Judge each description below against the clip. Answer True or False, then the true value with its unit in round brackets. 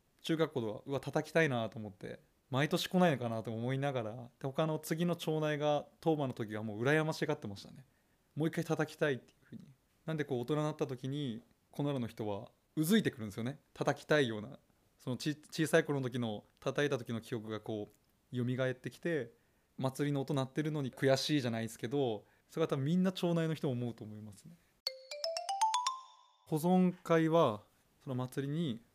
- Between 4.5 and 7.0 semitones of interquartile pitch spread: True (5.2 semitones)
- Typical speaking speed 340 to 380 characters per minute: True (375 characters per minute)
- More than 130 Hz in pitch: True (140 Hz)